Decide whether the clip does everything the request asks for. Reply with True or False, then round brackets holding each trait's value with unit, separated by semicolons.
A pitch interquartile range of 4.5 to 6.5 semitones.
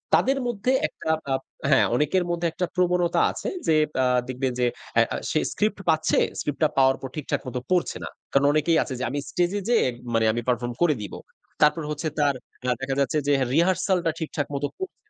True (4.8 semitones)